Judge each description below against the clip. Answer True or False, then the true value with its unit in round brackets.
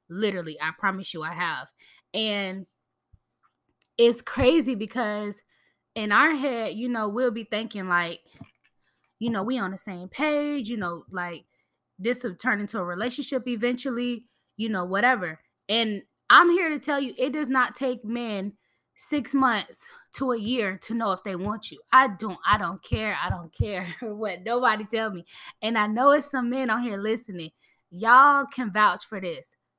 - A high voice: True (225 Hz)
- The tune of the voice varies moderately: True (4.6 semitones)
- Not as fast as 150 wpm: False (175 wpm)